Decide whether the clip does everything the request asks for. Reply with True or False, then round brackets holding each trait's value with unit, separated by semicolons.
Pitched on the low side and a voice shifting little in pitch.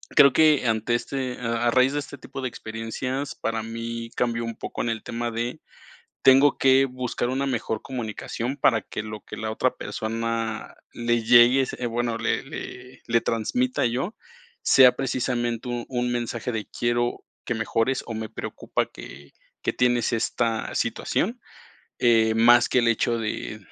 True (120 Hz; 1.9 semitones)